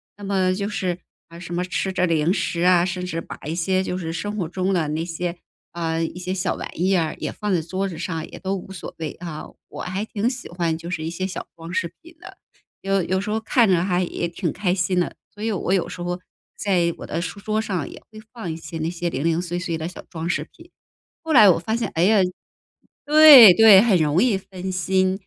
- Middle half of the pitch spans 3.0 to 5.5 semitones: No, narrow, 2.6 semitones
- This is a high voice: No, medium, 180 Hz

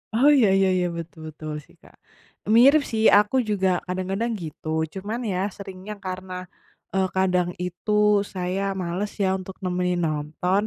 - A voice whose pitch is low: No, medium, 185 Hz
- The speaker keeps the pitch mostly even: Yes, narrow, 2.1 semitones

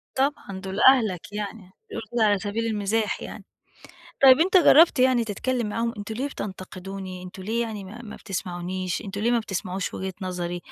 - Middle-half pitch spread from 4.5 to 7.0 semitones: No, average, 3.8 semitones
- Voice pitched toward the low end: No, high, 205 Hz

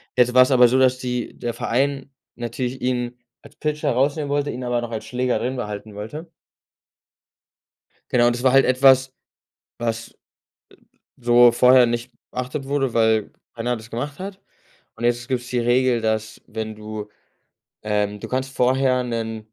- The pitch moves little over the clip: Yes, narrow, 2.1 semitones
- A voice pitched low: Yes, low, 125 Hz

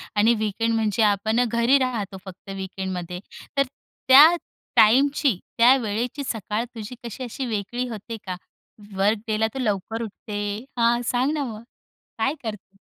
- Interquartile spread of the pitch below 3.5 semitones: Yes, average, 3.1 semitones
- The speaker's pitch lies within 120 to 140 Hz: No, high, 225 Hz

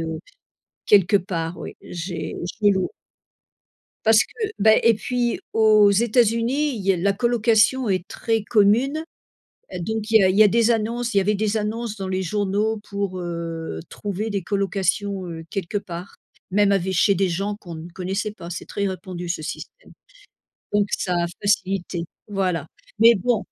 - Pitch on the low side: No, high, 200 Hz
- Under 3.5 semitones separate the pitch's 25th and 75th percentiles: Yes, average, 3.1 semitones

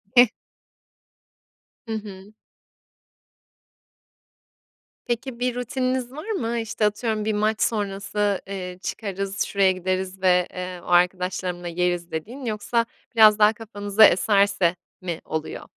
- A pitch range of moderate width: Yes, average, 3.6 semitones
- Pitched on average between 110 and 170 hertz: No, high, 205 Hz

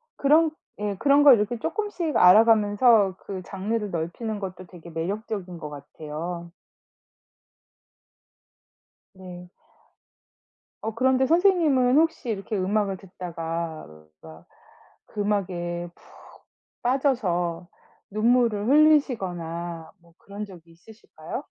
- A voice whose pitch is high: Yes, high, 200 Hz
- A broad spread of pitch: Yes, wide, 5.8 semitones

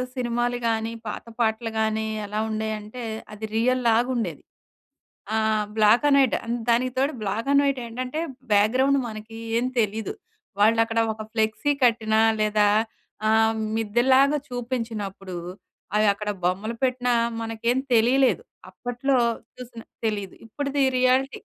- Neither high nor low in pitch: No, high, 230 Hz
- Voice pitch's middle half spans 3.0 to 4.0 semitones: No, narrow, 2.5 semitones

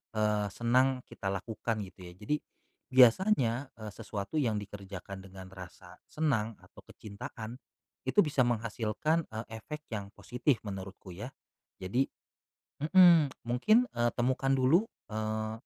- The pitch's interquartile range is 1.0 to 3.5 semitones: No, average, 4.3 semitones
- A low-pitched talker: Yes, low, 115 Hz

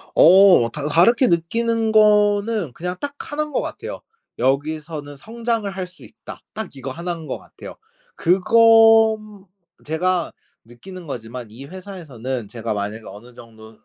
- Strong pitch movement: Yes, wide, 8.3 semitones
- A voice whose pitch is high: No, medium, 175 Hz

